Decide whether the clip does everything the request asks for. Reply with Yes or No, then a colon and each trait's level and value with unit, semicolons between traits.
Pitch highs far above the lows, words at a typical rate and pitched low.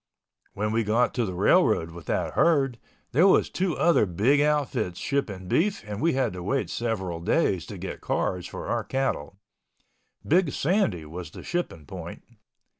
Yes: wide, 8.2 semitones; average, 170 wpm; low, 115 Hz